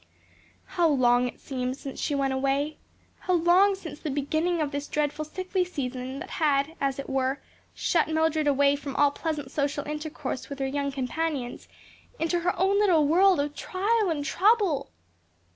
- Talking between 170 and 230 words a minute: Yes, average, 175 wpm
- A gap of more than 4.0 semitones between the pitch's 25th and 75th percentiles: No, average, 3.4 semitones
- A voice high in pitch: Yes, very high, 295 Hz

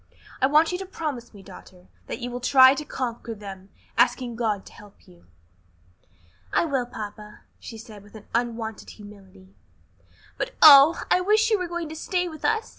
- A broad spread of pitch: Yes, wide, 7.2 semitones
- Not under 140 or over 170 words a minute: No, average, 180 wpm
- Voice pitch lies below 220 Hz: No, high, 240 Hz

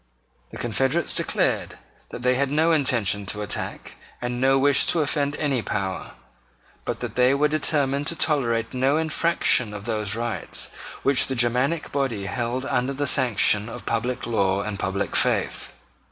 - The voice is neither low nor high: No, low, 125 Hz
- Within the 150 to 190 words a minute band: Yes, average, 160 wpm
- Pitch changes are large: No, average, 3.8 semitones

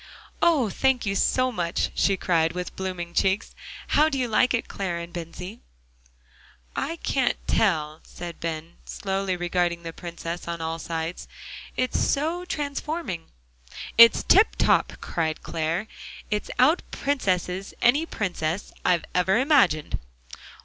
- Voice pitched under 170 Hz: No, medium, 185 Hz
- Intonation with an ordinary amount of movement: No, wide, 7.0 semitones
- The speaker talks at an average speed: No, slow, 130 wpm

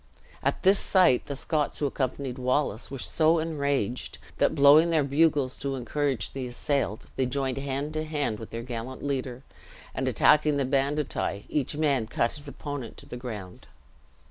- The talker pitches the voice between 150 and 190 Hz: No, medium, 140 Hz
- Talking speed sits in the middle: Yes, average, 170 wpm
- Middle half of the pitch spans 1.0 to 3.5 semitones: Yes, average, 2.9 semitones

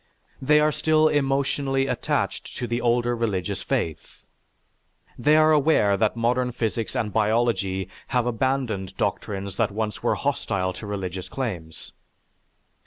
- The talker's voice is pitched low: Yes, low, 115 Hz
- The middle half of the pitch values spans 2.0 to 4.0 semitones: No, average, 5.2 semitones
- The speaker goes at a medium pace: No, slow, 130 wpm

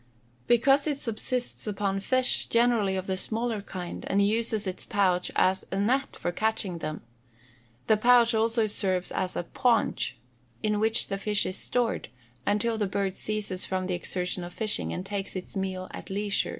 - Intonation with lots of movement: No, average, 3.4 semitones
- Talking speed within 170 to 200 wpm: Yes, average, 175 wpm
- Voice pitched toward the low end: No, high, 205 Hz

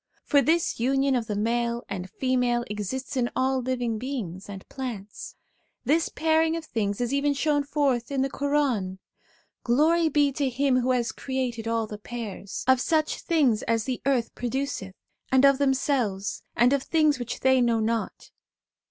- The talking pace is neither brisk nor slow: Yes, average, 170 wpm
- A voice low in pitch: No, very high, 255 Hz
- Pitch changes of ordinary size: Yes, average, 3.4 semitones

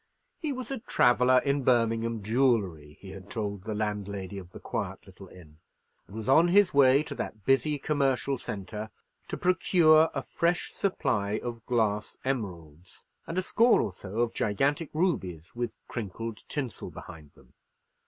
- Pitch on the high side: No, low, 115 Hz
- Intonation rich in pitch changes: Yes, wide, 5.9 semitones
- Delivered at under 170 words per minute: Yes, average, 155 wpm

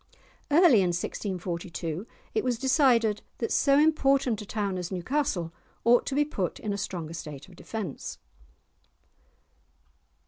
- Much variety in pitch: Yes, wide, 7.1 semitones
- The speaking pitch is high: Yes, high, 210 Hz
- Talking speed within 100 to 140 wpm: Yes, slow, 135 wpm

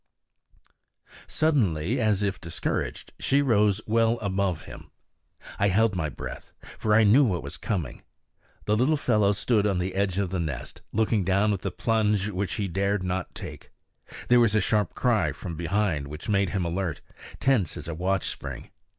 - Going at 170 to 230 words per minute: Yes, average, 175 wpm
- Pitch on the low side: Yes, low, 100 Hz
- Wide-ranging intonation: No, average, 3.3 semitones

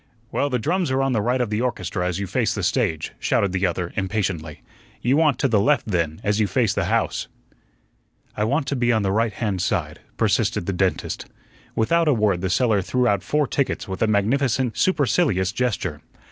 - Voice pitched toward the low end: Yes, low, 110 Hz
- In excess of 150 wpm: Yes, fast, 205 wpm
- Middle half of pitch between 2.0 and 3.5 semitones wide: No, average, 5.2 semitones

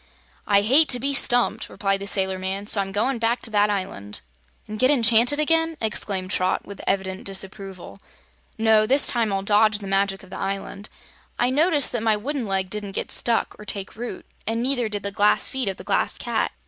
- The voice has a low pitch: No, high, 210 Hz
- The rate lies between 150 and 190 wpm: No, fast, 205 wpm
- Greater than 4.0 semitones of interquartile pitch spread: No, average, 3.7 semitones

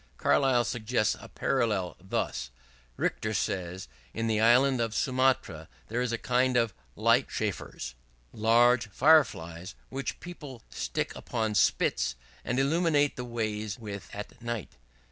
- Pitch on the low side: Yes, low, 115 Hz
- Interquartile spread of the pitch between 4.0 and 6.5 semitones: No, average, 3.5 semitones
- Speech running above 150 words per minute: No, slow, 135 wpm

